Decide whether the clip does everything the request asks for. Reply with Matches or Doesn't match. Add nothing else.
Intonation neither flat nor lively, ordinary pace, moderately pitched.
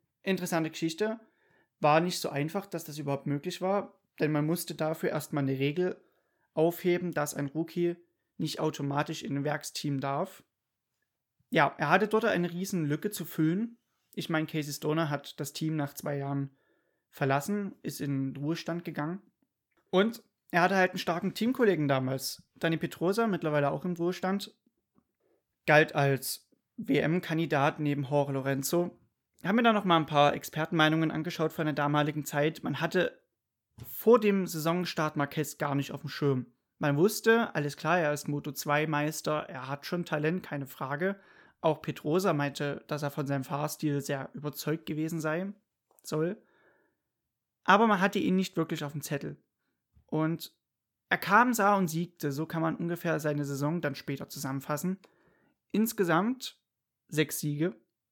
Matches